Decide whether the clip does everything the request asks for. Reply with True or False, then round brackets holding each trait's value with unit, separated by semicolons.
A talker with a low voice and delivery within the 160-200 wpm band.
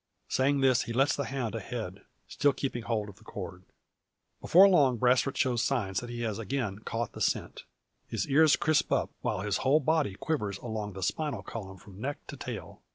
True (120 Hz; 190 wpm)